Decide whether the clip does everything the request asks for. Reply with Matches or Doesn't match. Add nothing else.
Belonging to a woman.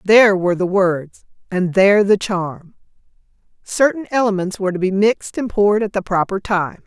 Matches